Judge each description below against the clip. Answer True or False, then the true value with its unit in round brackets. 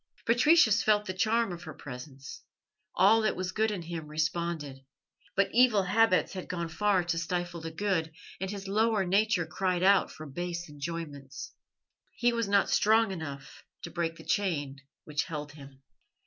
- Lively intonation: False (4.5 semitones)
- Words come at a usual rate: True (165 wpm)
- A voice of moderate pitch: True (175 Hz)